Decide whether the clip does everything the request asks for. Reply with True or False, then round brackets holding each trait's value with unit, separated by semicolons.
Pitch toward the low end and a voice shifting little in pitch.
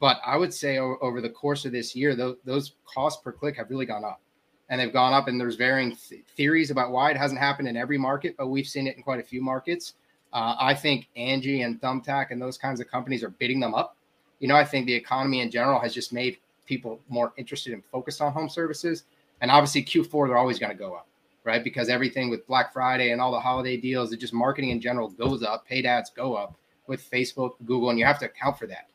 True (130 Hz; 2.2 semitones)